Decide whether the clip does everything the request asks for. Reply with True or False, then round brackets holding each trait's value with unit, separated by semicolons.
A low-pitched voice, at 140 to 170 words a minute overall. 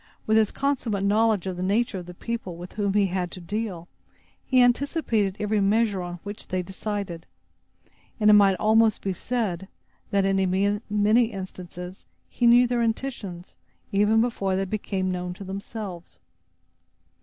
False (200 Hz; 155 wpm)